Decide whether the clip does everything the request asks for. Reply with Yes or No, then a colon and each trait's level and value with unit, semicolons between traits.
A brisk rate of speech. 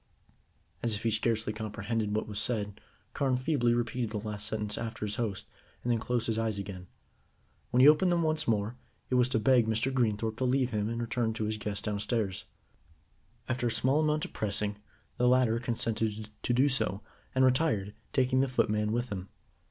No: average, 190 wpm